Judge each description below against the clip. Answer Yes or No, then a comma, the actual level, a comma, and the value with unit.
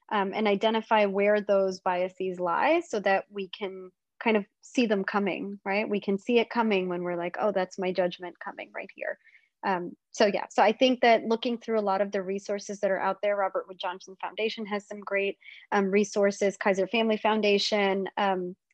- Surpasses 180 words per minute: Yes, average, 200 wpm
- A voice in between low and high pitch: No, high, 200 Hz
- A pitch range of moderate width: No, narrow, 2.1 semitones